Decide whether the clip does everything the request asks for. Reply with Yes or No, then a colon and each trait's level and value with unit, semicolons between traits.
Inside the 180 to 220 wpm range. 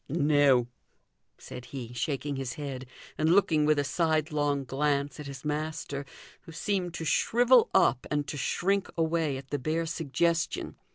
No: average, 155 wpm